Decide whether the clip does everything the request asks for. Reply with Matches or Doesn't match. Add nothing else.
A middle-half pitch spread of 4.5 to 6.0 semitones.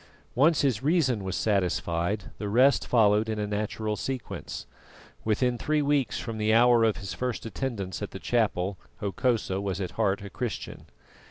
Doesn't match